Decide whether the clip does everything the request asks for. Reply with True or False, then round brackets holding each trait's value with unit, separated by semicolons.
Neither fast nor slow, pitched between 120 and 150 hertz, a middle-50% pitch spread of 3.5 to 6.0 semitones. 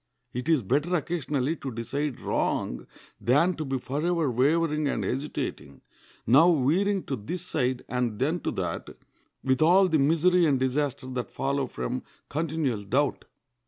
True (150 wpm; 140 Hz; 4.1 semitones)